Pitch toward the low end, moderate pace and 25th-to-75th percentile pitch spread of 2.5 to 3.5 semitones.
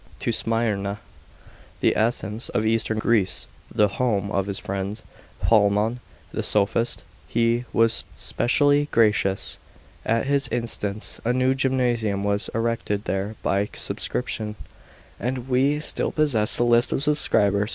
No: low, 115 Hz; slow, 130 wpm; average, 3.1 semitones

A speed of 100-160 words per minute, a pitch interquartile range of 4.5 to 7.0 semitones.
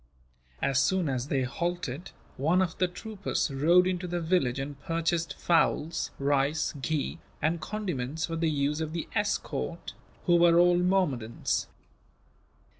No: average, 140 wpm; average, 4.1 semitones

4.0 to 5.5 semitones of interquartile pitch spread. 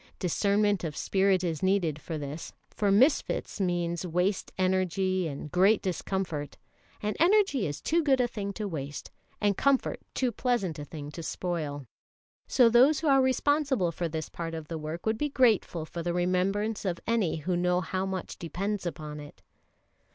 Yes: average, 4.5 semitones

